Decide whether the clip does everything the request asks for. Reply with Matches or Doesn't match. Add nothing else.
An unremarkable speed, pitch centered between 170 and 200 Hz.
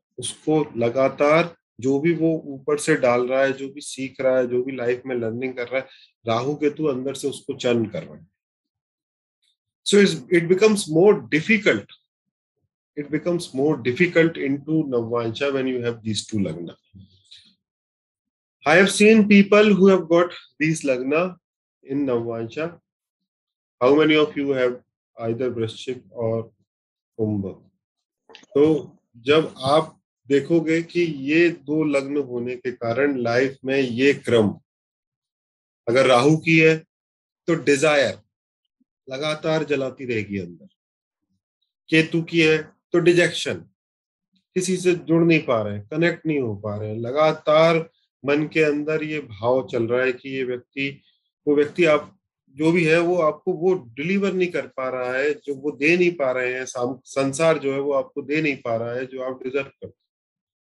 Doesn't match